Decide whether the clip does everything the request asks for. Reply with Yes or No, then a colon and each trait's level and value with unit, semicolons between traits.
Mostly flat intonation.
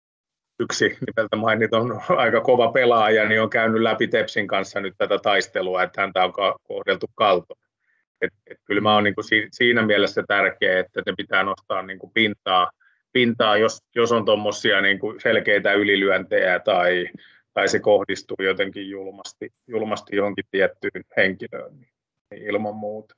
Yes: narrow, 2.3 semitones